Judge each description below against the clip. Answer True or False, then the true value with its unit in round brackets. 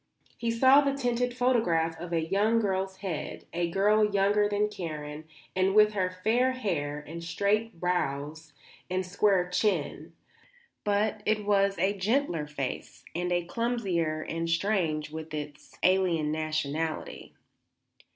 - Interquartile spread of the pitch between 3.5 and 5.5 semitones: True (4.6 semitones)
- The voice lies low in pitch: False (185 Hz)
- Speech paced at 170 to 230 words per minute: False (135 wpm)